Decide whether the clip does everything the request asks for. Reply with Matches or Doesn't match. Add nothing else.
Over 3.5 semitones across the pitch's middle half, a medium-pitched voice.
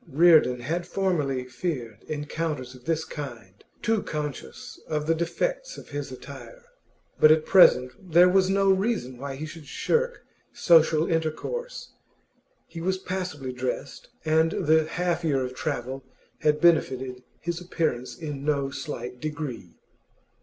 Matches